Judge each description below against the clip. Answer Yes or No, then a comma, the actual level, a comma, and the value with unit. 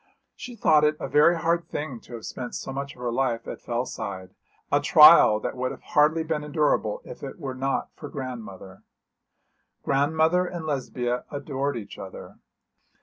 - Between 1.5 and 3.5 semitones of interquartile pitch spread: No, average, 4.3 semitones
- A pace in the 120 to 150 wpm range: No, average, 170 wpm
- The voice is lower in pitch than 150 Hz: Yes, medium, 140 Hz